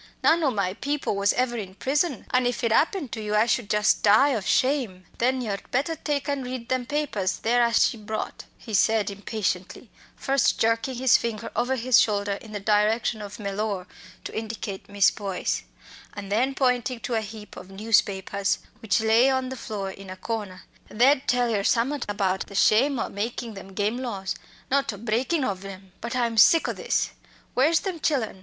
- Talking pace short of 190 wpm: No, average, 195 wpm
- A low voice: No, high, 225 Hz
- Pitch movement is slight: No, average, 4.0 semitones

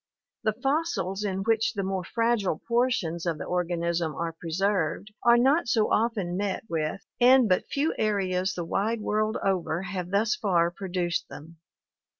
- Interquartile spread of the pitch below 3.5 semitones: No, average, 4.4 semitones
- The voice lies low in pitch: No, high, 195 Hz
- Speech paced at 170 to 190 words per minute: No, average, 155 wpm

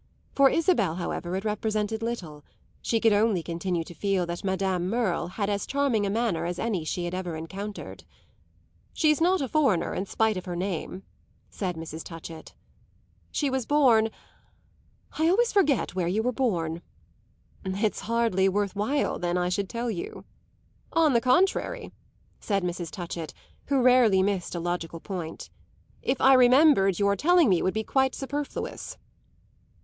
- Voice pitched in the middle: No, high, 200 Hz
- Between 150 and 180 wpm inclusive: Yes, average, 160 wpm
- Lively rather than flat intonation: Yes, wide, 5.9 semitones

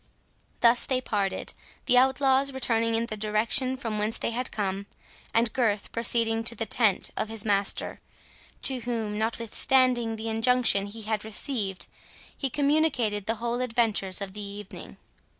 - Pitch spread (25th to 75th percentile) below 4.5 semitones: Yes, average, 3.0 semitones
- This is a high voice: Yes, high, 225 Hz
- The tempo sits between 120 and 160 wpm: Yes, average, 150 wpm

